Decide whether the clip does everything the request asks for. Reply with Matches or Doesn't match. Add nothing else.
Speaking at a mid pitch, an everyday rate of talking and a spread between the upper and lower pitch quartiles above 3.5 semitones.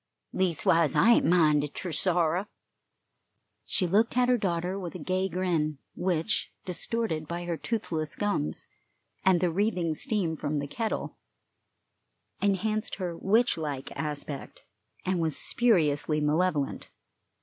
Doesn't match